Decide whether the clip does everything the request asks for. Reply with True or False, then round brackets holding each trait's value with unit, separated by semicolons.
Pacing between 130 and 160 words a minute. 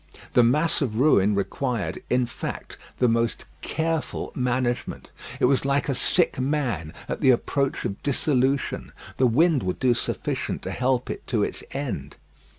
True (155 wpm)